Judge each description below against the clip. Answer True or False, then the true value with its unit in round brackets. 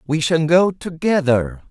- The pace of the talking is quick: False (140 wpm)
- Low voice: False (155 Hz)